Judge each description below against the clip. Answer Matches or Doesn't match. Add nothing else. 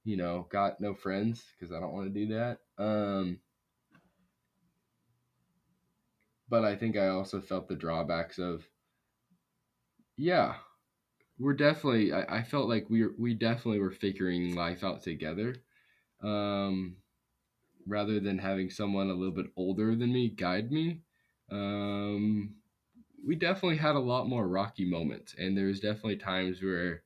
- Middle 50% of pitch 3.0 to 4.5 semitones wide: Matches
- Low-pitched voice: Matches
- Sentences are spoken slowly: Doesn't match